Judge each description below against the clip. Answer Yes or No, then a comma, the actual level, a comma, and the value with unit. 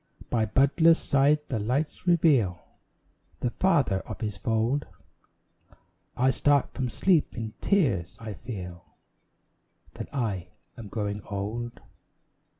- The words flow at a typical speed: No, slow, 115 wpm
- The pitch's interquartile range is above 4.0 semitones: Yes, wide, 5.5 semitones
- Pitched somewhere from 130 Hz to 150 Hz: No, low, 120 Hz